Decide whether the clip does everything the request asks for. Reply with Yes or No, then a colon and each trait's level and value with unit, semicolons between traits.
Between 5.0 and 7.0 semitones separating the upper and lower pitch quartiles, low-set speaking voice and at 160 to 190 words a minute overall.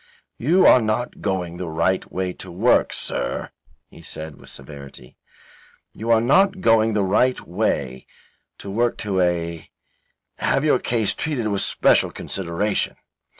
No: average, 5.3 semitones; low, 100 Hz; average, 145 wpm